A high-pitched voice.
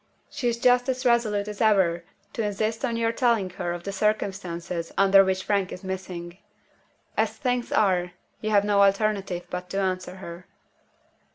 Yes: high, 200 Hz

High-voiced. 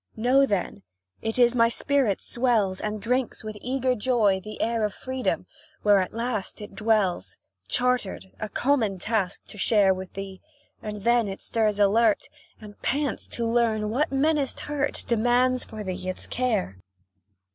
Yes: high, 225 Hz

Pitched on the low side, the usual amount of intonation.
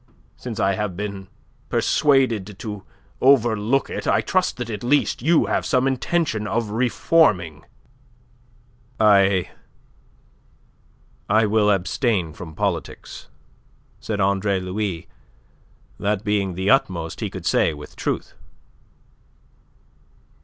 Yes: low, 105 Hz; average, 4.0 semitones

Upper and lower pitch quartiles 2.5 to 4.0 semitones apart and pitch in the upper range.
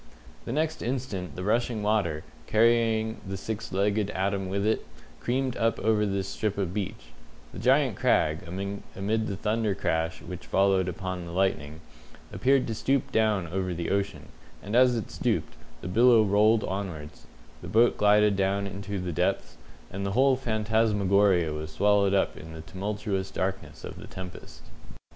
No: average, 2.8 semitones; low, 100 Hz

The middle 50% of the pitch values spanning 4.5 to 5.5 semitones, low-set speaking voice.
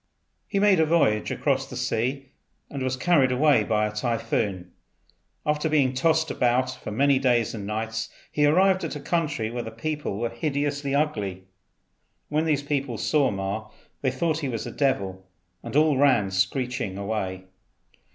Yes: average, 5.2 semitones; low, 130 Hz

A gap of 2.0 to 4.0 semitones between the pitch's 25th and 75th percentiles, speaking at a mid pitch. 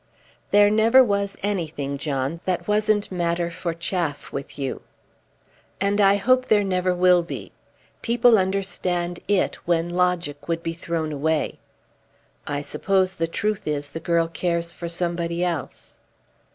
Yes: average, 3.1 semitones; medium, 175 Hz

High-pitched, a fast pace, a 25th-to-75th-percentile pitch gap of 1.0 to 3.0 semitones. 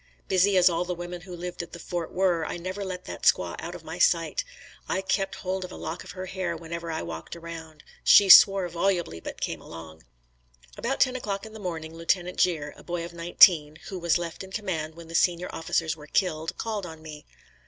No: medium, 175 Hz; fast, 220 wpm; narrow, 2.5 semitones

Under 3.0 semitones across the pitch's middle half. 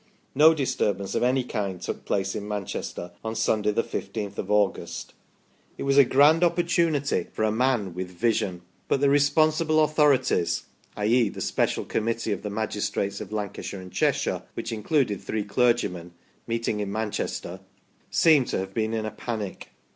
No: average, 5.1 semitones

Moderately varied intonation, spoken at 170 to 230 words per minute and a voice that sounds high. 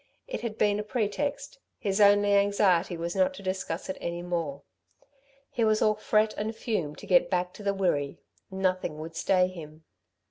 Yes: average, 3.5 semitones; average, 180 wpm; high, 195 Hz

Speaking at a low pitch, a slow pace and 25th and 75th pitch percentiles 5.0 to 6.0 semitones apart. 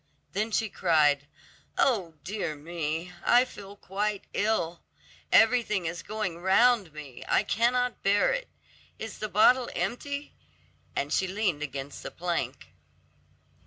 No: high, 195 Hz; slow, 125 wpm; average, 5.3 semitones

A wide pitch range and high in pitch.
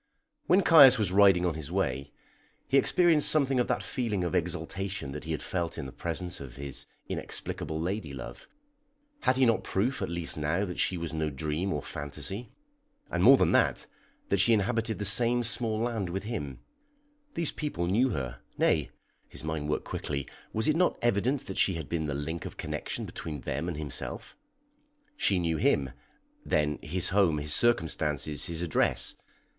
No: wide, 6.9 semitones; very low, 90 Hz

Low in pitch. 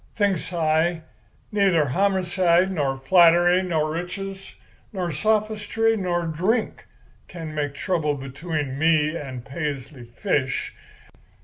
No: medium, 170 Hz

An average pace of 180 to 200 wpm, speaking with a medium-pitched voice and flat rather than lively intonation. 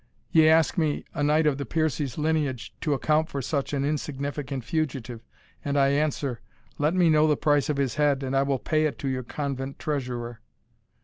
Yes: average, 195 wpm; medium, 145 Hz; narrow, 2.3 semitones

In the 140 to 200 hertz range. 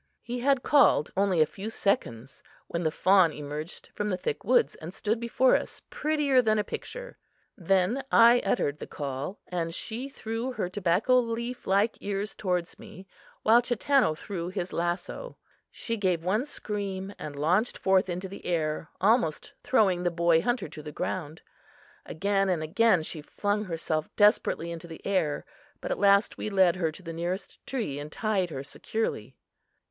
Yes: high, 190 Hz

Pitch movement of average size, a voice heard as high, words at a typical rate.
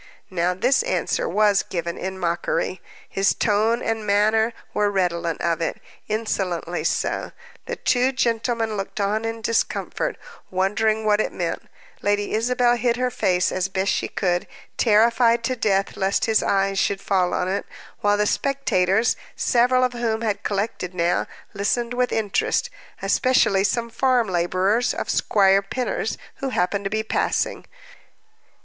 Yes: average, 3.4 semitones; high, 210 Hz; average, 150 wpm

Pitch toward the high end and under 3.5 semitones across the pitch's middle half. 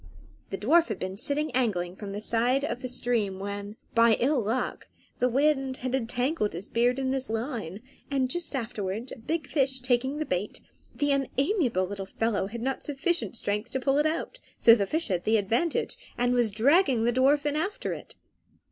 No: high, 245 Hz; average, 4.6 semitones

